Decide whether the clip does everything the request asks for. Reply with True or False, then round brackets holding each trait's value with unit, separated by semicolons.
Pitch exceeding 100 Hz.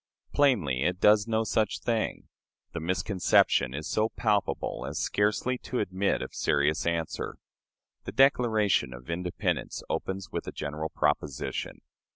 False (95 Hz)